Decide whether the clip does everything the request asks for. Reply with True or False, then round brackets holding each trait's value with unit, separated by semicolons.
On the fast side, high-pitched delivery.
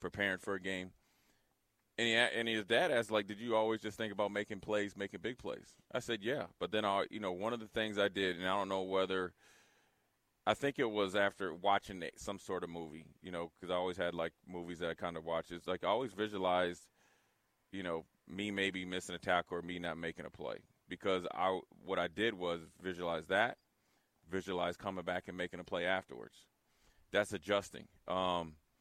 False (210 wpm; 95 Hz)